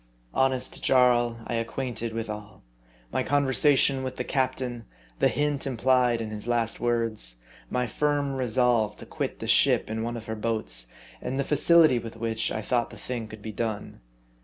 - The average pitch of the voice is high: No, low, 120 Hz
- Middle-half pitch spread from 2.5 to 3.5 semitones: Yes, average, 2.8 semitones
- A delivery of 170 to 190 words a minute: Yes, average, 180 wpm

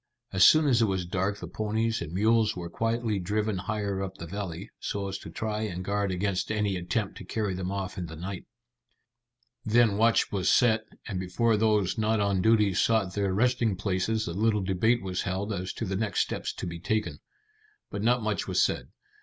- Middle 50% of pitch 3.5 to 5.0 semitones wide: No, average, 2.9 semitones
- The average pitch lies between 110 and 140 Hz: No, low, 100 Hz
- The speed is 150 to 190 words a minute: No, fast, 205 wpm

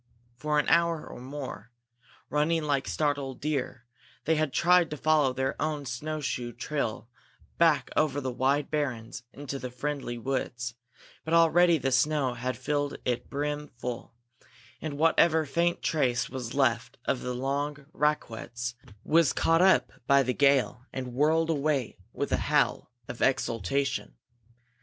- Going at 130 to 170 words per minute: Yes, average, 145 wpm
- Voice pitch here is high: No, medium, 140 Hz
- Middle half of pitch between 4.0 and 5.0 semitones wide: No, average, 3.3 semitones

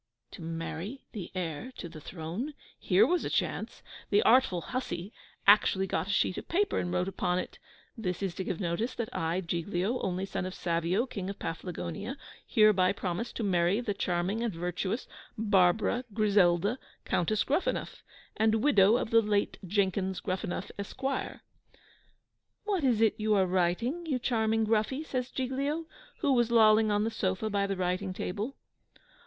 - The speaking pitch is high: Yes, high, 200 Hz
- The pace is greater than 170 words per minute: No, average, 165 wpm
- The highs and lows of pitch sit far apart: No, average, 4.4 semitones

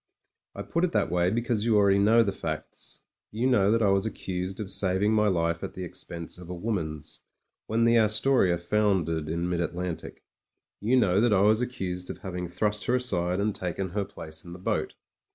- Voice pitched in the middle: No, very low, 95 Hz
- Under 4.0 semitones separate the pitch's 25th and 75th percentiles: Yes, average, 3.4 semitones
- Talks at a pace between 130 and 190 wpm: No, fast, 205 wpm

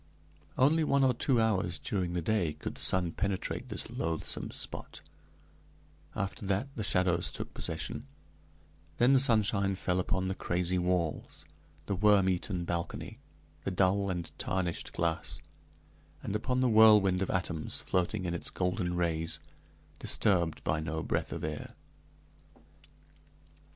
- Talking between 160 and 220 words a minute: No, average, 140 wpm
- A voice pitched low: Yes, very low, 95 Hz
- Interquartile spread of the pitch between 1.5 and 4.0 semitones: Yes, average, 3.3 semitones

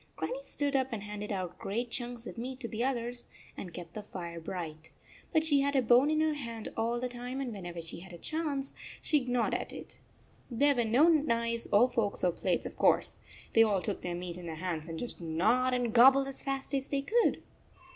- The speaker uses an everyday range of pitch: No, wide, 6.1 semitones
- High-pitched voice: Yes, high, 235 Hz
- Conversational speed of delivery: No, fast, 220 wpm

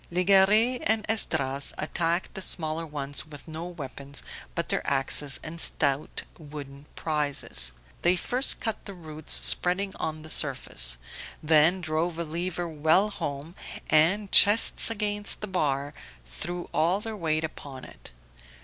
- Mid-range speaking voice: Yes, medium, 160 Hz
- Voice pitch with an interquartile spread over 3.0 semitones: Yes, average, 4.4 semitones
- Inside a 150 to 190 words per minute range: No, average, 140 wpm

